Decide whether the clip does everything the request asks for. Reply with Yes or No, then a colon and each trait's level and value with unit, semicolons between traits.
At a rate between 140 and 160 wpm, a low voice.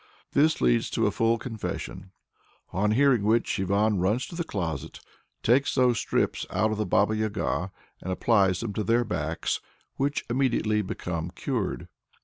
Yes: average, 155 wpm; low, 110 Hz